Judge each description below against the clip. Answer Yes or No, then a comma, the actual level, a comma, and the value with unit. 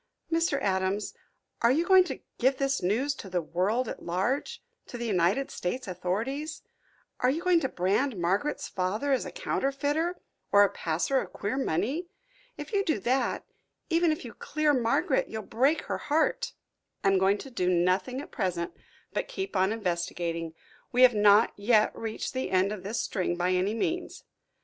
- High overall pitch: Yes, high, 225 Hz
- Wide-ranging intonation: Yes, wide, 7.0 semitones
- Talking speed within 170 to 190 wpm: Yes, average, 180 wpm